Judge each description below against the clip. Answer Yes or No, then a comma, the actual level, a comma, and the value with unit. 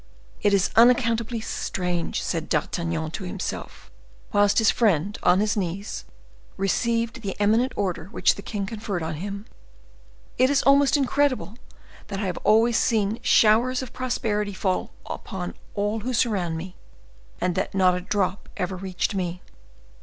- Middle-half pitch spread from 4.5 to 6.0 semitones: No, average, 3.9 semitones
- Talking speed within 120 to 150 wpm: Yes, average, 145 wpm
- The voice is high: Yes, high, 205 Hz